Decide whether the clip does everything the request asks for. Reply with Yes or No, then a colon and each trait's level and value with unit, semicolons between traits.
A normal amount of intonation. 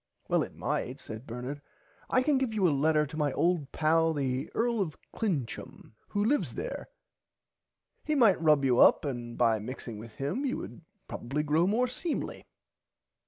No: wide, 8.4 semitones